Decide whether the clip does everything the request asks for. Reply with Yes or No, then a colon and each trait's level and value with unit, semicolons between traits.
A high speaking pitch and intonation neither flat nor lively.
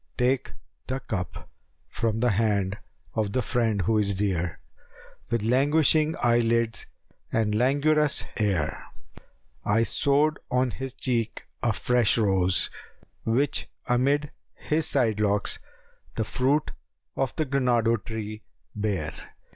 No: low, 115 Hz; average, 4.0 semitones